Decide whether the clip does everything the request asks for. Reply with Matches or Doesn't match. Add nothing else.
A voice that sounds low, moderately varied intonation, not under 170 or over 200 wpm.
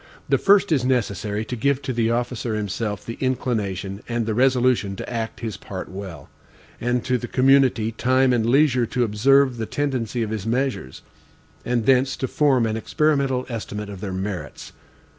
Matches